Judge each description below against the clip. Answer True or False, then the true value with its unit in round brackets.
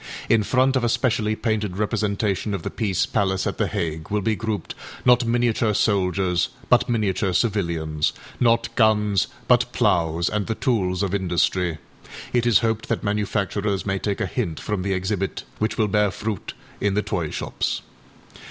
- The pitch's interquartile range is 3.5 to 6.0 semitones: False (2.9 semitones)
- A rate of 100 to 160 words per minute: False (170 wpm)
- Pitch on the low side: True (105 Hz)